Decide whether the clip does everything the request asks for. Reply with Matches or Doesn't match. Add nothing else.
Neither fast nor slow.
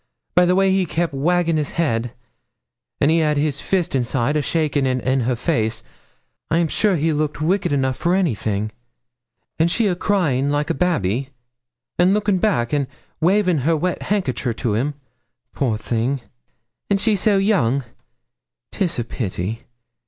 Matches